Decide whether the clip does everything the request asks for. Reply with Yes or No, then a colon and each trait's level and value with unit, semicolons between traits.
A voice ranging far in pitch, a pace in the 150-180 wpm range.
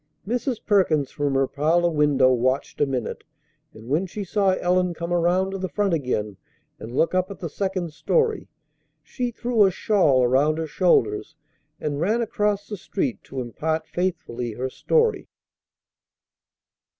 Yes: wide, 6.1 semitones; average, 155 wpm